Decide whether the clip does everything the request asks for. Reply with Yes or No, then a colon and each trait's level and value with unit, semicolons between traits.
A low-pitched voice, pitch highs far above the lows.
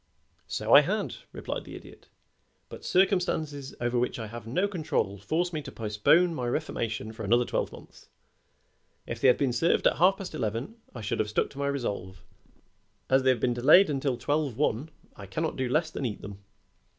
Yes: low, 130 Hz; wide, 5.7 semitones